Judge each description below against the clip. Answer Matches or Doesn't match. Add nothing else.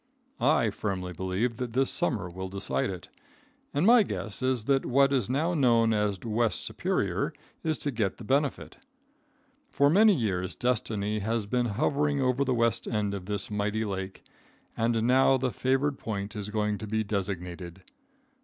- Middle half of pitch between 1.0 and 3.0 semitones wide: Doesn't match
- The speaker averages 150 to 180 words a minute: Matches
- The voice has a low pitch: Matches